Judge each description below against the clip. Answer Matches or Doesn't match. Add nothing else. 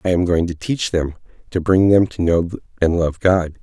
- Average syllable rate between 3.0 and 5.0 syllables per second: Matches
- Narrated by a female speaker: Doesn't match